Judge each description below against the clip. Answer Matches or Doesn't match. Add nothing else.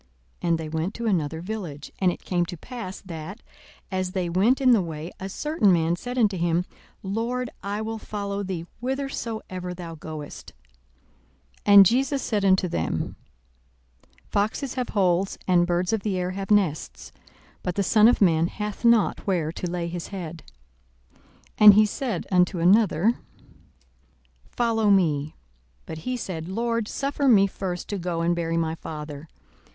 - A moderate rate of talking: Matches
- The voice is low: Doesn't match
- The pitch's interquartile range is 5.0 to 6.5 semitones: Doesn't match